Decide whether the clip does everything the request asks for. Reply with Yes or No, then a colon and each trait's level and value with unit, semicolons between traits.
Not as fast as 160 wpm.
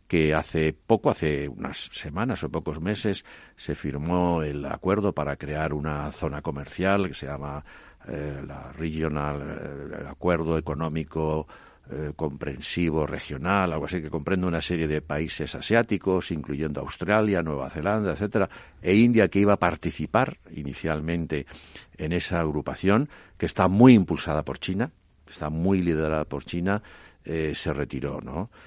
Yes: average, 145 wpm